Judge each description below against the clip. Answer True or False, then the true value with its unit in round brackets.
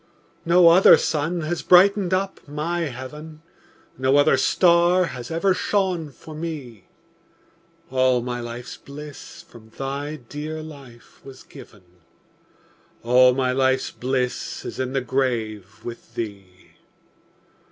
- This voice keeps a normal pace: False (120 wpm)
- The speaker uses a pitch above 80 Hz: True (135 Hz)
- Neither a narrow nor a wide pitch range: True (4.8 semitones)